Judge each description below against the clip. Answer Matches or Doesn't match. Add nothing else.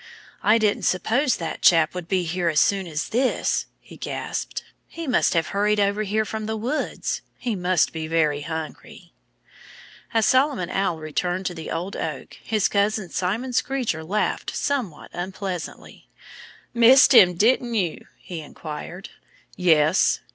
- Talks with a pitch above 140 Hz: Matches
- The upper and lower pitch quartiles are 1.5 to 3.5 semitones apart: Doesn't match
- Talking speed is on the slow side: Doesn't match